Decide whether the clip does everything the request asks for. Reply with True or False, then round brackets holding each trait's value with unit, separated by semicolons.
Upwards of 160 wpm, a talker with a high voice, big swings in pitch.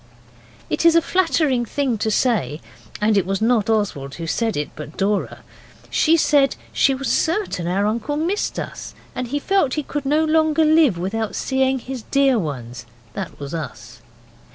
True (175 wpm; 240 Hz; 7.3 semitones)